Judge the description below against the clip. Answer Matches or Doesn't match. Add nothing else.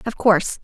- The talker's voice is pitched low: Doesn't match